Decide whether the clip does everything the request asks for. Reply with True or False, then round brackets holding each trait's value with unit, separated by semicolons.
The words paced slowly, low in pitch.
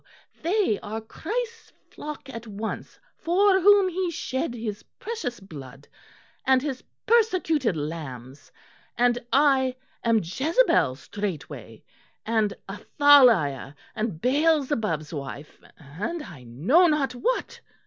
False (105 wpm; 240 Hz)